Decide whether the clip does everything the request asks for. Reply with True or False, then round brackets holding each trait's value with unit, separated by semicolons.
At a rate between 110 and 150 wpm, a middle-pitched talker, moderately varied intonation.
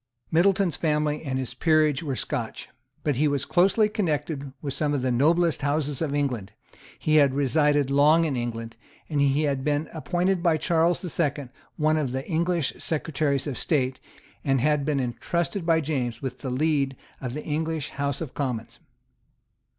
False (170 wpm; 145 Hz; 3.0 semitones)